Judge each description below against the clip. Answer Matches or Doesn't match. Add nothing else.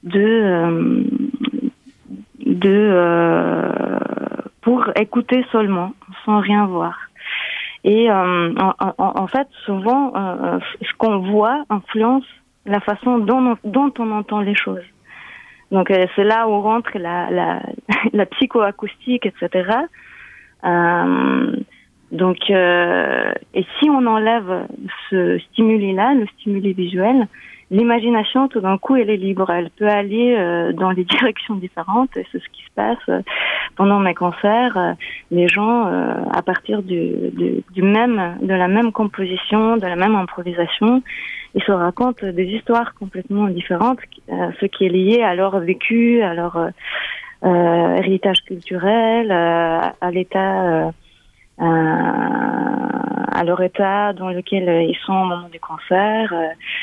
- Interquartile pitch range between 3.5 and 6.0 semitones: Matches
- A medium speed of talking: Doesn't match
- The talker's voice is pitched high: Matches